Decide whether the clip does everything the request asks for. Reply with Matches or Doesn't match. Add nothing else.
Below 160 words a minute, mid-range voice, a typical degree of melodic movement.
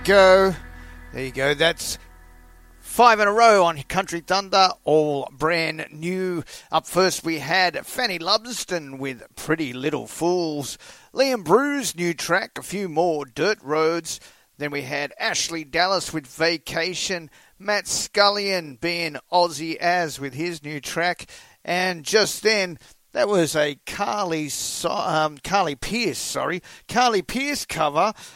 Matches